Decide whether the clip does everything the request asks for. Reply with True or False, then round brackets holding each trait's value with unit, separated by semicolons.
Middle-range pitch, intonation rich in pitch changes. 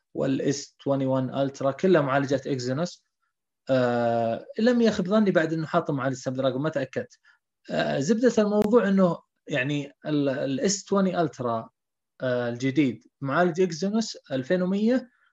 True (155 Hz; 6.6 semitones)